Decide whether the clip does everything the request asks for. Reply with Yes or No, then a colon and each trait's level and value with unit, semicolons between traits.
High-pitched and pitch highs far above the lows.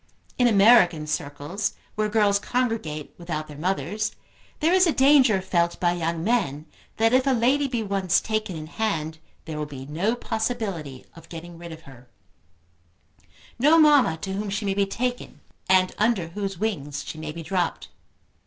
Yes: high, 195 Hz; wide, 5.7 semitones